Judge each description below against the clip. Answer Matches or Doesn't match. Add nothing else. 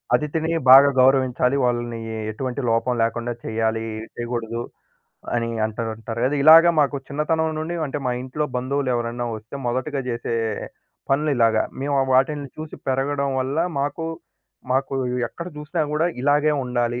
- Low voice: Matches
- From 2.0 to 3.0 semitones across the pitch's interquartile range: Doesn't match